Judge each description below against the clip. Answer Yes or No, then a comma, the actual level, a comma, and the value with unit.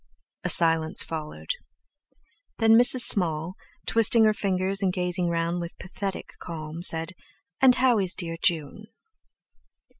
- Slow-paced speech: Yes, slow, 125 wpm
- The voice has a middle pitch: Yes, medium, 180 Hz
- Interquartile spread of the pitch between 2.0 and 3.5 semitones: No, average, 4.1 semitones